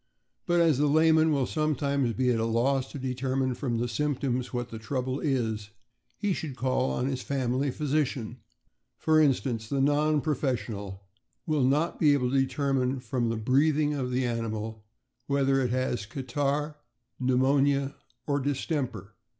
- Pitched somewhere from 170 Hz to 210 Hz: No, low, 135 Hz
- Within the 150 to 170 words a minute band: Yes, average, 160 wpm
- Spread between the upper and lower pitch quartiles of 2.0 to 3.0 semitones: Yes, average, 2.7 semitones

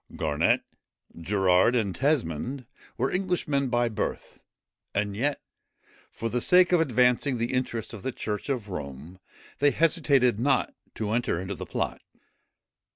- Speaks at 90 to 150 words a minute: Yes, average, 140 wpm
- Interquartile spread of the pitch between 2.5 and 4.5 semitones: No, wide, 5.5 semitones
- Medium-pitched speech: No, low, 120 Hz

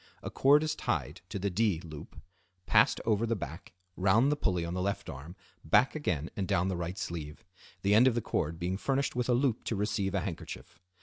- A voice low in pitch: Yes, low, 100 Hz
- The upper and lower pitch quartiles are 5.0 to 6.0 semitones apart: Yes, average, 5.3 semitones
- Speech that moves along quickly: Yes, fast, 220 wpm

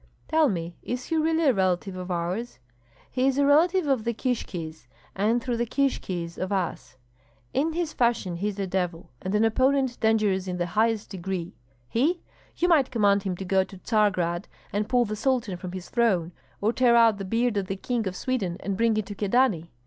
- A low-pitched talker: No, high, 210 Hz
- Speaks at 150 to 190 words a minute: No, fast, 205 wpm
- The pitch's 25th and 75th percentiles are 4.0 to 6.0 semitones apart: Yes, average, 5.0 semitones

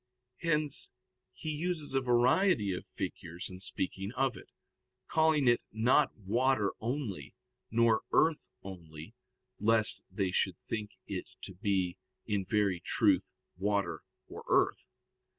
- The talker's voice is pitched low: Yes, low, 110 Hz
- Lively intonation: Yes, wide, 5.8 semitones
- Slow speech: Yes, slow, 125 wpm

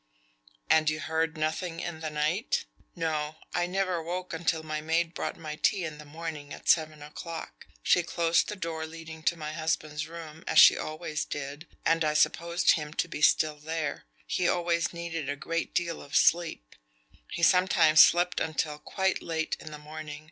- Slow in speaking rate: No, average, 180 wpm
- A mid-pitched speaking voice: Yes, medium, 160 Hz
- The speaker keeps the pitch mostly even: Yes, narrow, 1.8 semitones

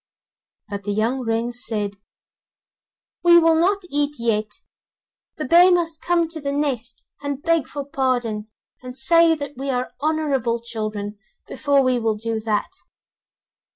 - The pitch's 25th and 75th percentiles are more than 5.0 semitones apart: Yes, wide, 5.5 semitones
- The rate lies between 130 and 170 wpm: Yes, average, 145 wpm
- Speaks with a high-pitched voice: Yes, very high, 265 Hz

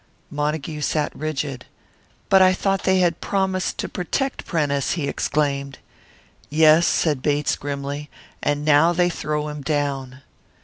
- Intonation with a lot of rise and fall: No, average, 3.1 semitones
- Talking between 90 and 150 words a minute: Yes, slow, 135 wpm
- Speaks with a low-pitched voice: No, medium, 150 Hz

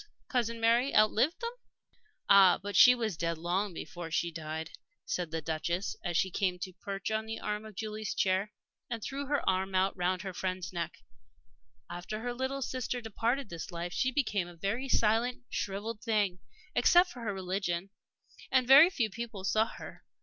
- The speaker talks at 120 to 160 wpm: No, average, 175 wpm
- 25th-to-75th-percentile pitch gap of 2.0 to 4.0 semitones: No, average, 4.6 semitones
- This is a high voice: Yes, high, 205 Hz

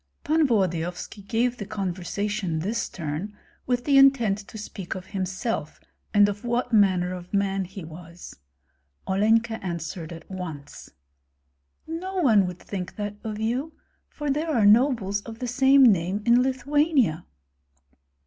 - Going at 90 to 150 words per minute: Yes, average, 140 wpm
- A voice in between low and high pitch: No, high, 205 Hz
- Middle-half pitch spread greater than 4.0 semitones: Yes, average, 5.0 semitones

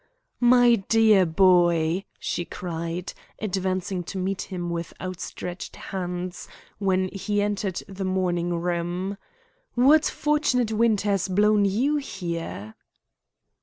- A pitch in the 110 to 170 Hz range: No, high, 190 Hz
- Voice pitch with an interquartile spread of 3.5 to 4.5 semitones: No, average, 3.0 semitones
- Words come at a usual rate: No, slow, 110 wpm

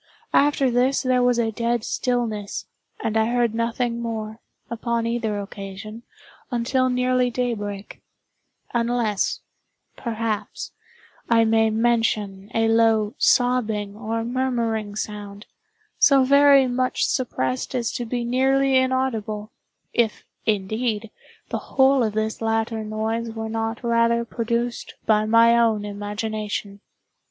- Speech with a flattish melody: Yes, narrow, 2.2 semitones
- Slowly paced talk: Yes, slow, 115 wpm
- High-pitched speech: Yes, high, 230 Hz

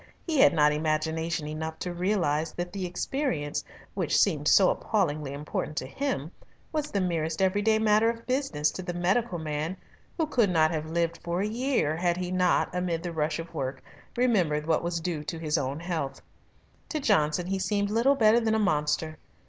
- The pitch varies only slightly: No, average, 5.1 semitones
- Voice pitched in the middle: Yes, medium, 175 Hz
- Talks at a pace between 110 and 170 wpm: No, average, 190 wpm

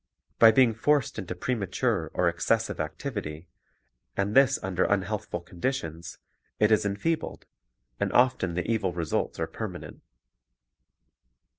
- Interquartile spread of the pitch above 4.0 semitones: Yes, average, 4.8 semitones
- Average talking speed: No, slow, 120 wpm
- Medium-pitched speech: No, low, 100 Hz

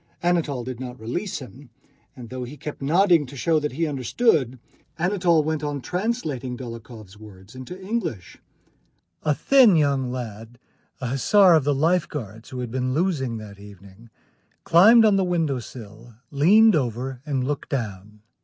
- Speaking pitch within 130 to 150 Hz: Yes, low, 135 Hz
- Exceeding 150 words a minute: Yes, average, 160 wpm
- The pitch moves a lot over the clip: Yes, wide, 5.9 semitones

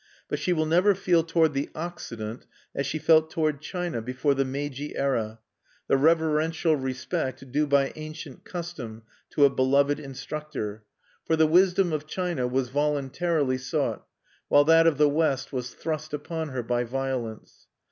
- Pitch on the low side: No, medium, 145 Hz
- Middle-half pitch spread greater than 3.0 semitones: Yes, average, 3.5 semitones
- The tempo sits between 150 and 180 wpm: Yes, average, 155 wpm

